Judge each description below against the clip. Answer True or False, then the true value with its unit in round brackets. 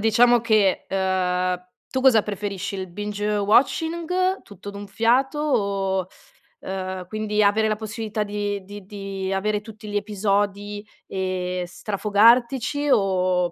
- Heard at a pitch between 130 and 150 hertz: False (205 Hz)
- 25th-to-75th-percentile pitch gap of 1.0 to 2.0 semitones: False (2.4 semitones)